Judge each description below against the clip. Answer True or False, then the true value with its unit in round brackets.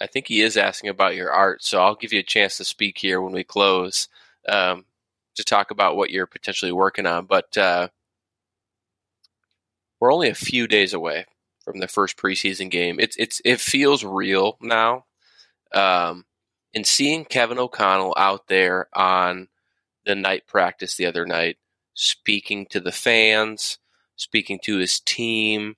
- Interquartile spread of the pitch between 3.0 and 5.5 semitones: True (3.3 semitones)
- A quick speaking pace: False (165 wpm)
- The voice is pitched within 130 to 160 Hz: False (100 Hz)